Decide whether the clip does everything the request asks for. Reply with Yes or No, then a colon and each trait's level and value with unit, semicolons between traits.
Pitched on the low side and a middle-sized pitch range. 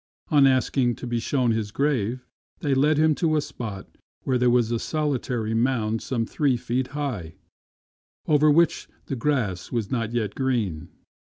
Yes: low, 125 Hz; average, 4.1 semitones